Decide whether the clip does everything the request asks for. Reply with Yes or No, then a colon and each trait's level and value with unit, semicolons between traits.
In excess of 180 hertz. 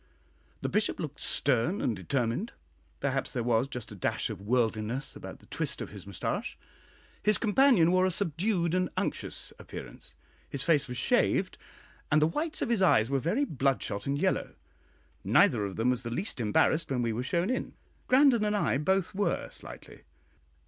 No: medium, 145 Hz